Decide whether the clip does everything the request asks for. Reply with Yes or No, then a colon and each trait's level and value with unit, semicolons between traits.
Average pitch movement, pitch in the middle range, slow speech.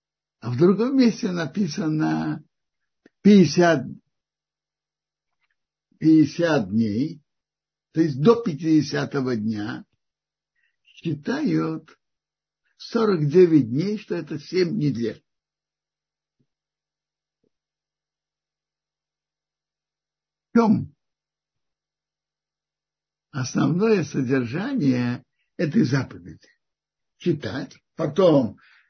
No: wide, 6.3 semitones; medium, 155 Hz; slow, 60 wpm